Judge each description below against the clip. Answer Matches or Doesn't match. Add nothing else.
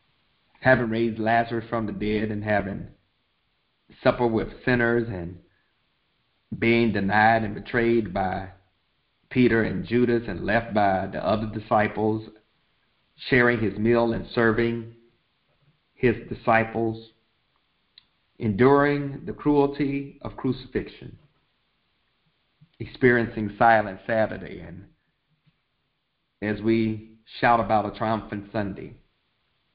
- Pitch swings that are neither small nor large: Doesn't match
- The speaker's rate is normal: Doesn't match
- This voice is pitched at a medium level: Doesn't match